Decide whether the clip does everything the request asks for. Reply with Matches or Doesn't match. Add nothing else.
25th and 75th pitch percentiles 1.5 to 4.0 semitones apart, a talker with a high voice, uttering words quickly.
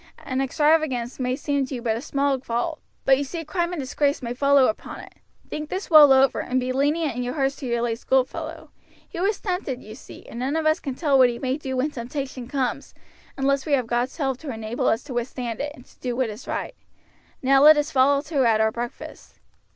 Matches